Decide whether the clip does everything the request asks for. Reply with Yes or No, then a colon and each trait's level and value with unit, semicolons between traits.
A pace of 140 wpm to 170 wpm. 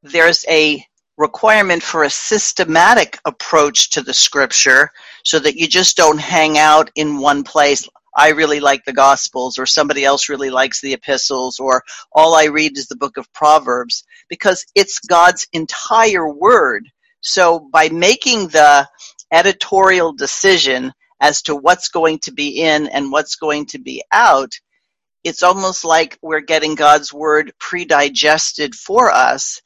Yes: average, 155 wpm